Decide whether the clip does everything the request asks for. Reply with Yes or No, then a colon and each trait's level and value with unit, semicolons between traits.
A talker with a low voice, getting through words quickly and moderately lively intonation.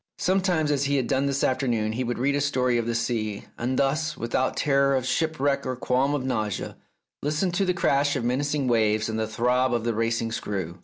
Yes: low, 130 Hz; fast, 215 wpm; average, 3.5 semitones